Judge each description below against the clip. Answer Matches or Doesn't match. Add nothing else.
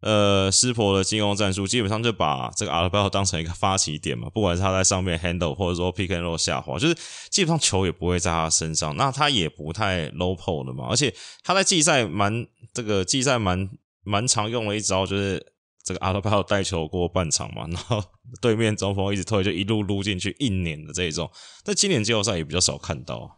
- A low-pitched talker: Matches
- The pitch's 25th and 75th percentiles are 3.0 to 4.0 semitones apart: Matches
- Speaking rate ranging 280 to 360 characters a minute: Doesn't match